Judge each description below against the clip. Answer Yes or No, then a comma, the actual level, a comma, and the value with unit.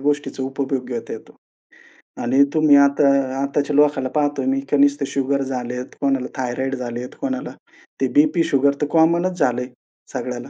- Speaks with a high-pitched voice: No, medium, 140 Hz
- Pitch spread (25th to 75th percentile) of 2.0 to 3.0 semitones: Yes, narrow, 2.5 semitones